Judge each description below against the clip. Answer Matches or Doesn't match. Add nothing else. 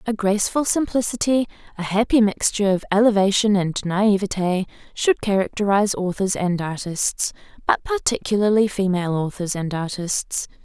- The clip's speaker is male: Doesn't match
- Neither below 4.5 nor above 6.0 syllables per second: Matches